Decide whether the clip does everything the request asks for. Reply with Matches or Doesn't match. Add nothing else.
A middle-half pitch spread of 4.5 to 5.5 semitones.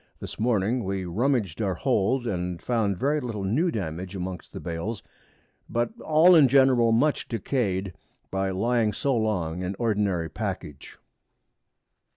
Matches